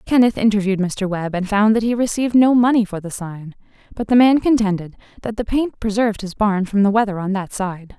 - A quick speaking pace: Yes, fast, 225 wpm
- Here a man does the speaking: No, female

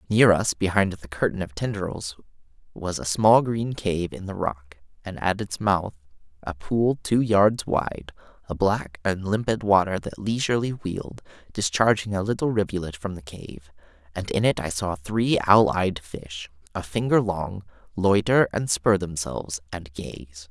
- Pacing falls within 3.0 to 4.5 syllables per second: Yes, 4.4 syllables/s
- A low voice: Yes, very low, 95 Hz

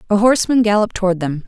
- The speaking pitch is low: No, high, 205 Hz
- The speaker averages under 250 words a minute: Yes, fast, 205 wpm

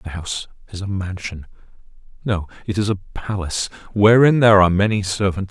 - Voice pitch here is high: No, low, 100 Hz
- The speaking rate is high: No, average, 165 wpm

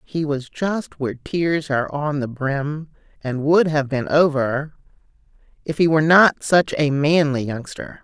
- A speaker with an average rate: Yes, average, 165 wpm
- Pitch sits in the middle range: Yes, medium, 150 Hz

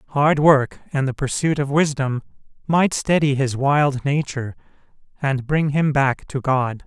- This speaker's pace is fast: No, average, 155 wpm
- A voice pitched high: No, medium, 140 Hz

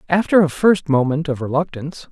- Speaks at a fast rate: No, average, 170 wpm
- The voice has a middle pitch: Yes, medium, 155 Hz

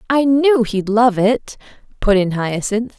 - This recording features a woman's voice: Yes, female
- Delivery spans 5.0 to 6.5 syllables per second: No, 3.8 syllables/s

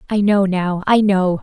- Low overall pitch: No, high, 195 Hz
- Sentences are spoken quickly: Yes, fast, 210 wpm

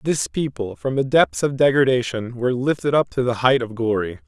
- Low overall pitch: Yes, low, 130 Hz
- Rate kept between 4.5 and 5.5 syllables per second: Yes, 5.4 syllables/s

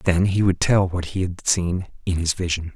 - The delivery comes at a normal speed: No, fast, 240 wpm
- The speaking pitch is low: Yes, very low, 90 Hz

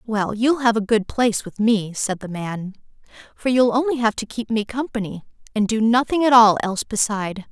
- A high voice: Yes, high, 220 Hz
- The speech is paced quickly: Yes, fast, 210 wpm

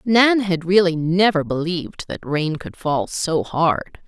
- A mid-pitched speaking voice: Yes, medium, 170 Hz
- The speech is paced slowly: No, average, 160 wpm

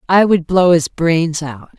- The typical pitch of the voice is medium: Yes, medium, 165 Hz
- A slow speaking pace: No, average, 200 wpm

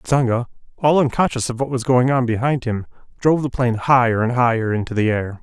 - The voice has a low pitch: Yes, low, 125 Hz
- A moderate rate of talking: No, fast, 210 wpm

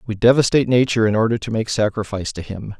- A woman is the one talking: No, male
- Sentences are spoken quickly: Yes, fast, 215 wpm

